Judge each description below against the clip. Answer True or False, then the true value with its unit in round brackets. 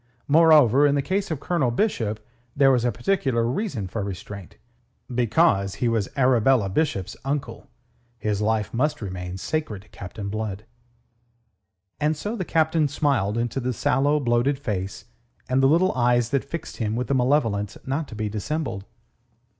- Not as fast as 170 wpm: True (160 wpm)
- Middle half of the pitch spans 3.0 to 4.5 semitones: False (5.5 semitones)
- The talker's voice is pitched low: True (125 Hz)